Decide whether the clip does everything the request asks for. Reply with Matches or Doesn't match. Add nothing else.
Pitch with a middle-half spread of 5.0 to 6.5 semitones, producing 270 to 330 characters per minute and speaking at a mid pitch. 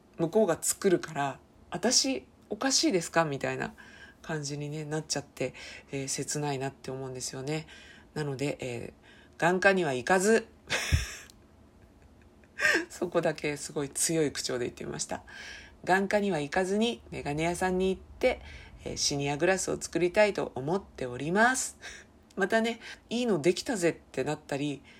Matches